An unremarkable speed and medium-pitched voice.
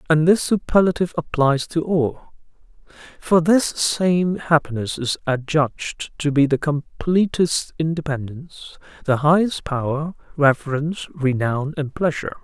No: slow, 115 wpm; medium, 155 Hz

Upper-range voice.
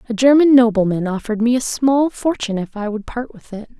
Yes: high, 235 Hz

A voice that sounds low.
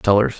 Yes: low, 105 Hz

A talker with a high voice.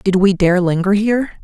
Yes: high, 195 Hz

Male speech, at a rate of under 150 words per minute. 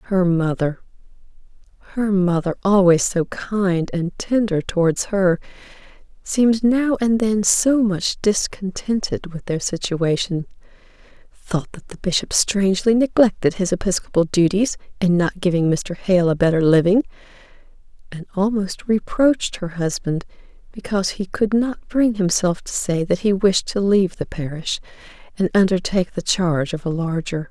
No: female; slow, 135 wpm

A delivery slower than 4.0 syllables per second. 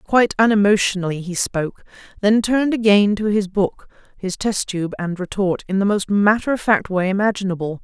No: 5.4 syllables/s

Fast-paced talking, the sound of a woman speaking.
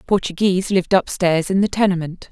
No: average, 155 wpm; female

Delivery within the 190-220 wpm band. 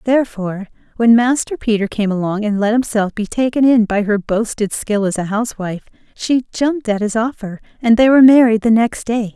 Yes: average, 200 wpm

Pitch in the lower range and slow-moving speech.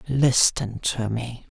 Yes: low, 120 Hz; slow, 115 wpm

